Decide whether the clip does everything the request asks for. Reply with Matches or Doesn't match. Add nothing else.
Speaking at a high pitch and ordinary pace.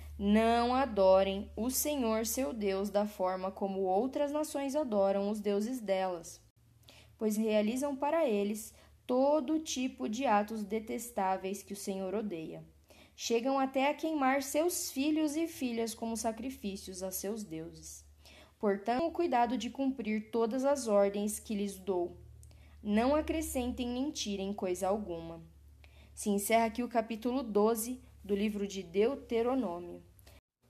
Matches